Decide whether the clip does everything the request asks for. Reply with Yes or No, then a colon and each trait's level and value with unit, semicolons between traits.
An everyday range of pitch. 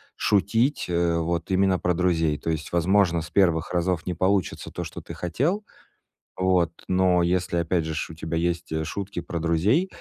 No: narrow, 2.2 semitones